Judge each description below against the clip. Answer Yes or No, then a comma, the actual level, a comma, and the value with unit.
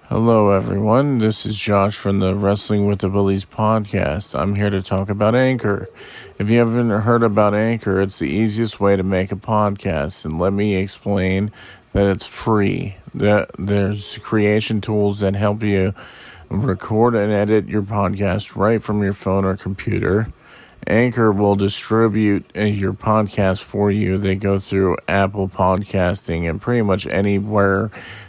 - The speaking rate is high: No, average, 155 wpm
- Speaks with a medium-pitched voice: No, low, 100 Hz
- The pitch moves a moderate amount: No, narrow, 1.9 semitones